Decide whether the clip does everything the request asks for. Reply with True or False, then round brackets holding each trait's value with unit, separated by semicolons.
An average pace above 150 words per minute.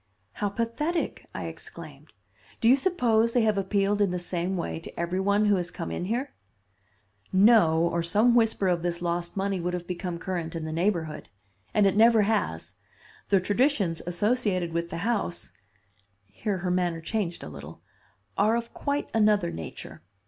True (170 wpm)